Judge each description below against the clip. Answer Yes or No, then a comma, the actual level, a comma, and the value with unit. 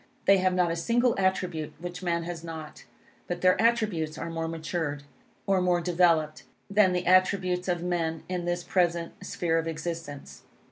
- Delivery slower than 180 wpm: Yes, average, 170 wpm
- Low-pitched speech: No, medium, 175 Hz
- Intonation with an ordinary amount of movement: No, narrow, 1.9 semitones